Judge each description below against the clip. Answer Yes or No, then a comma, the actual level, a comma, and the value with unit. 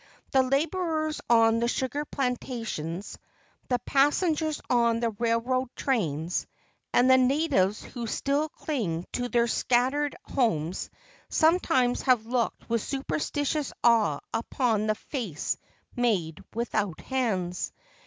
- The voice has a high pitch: Yes, high, 245 Hz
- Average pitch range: Yes, average, 3.9 semitones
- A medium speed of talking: No, slow, 115 wpm